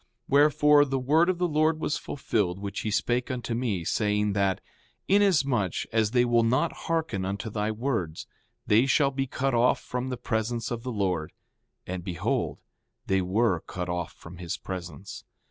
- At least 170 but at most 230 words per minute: Yes, average, 175 wpm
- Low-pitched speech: Yes, low, 115 Hz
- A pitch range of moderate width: No, wide, 5.8 semitones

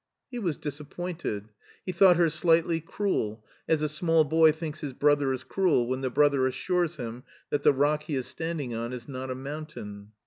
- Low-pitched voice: No, medium, 150 Hz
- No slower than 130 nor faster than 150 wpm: No, average, 195 wpm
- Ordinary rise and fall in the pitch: Yes, average, 4.1 semitones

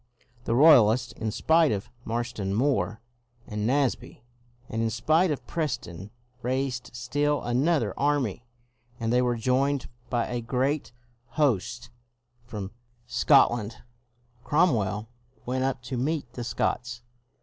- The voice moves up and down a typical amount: Yes, average, 3.5 semitones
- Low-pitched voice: Yes, low, 120 Hz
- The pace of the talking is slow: Yes, slow, 125 wpm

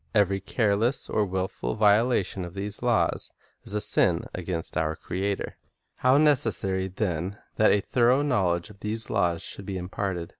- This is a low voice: Yes, low, 100 Hz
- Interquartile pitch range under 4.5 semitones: Yes, average, 3.0 semitones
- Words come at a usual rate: Yes, average, 160 wpm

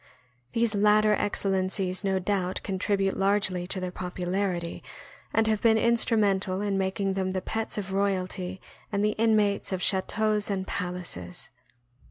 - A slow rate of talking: No, average, 145 wpm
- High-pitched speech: Yes, high, 195 Hz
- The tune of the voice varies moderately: No, narrow, 2.0 semitones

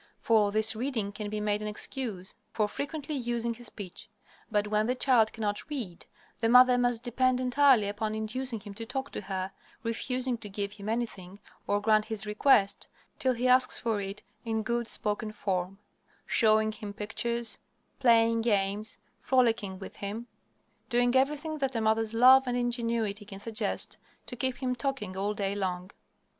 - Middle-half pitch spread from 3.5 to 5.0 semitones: No, average, 3.1 semitones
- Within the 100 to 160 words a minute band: No, average, 170 wpm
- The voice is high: Yes, high, 225 Hz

